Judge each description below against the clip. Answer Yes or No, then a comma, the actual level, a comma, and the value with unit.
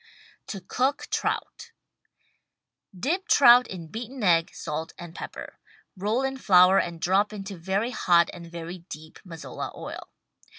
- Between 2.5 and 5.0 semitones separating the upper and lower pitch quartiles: No, wide, 5.5 semitones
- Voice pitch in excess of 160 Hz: Yes, high, 190 Hz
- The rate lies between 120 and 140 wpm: Yes, slow, 135 wpm